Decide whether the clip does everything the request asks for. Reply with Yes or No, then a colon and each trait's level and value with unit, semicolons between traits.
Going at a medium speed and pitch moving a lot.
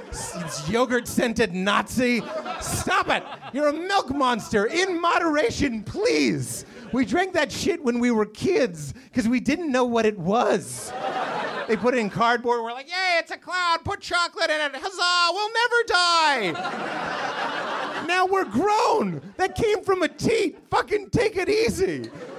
Yes: average, 155 wpm; wide, 7.7 semitones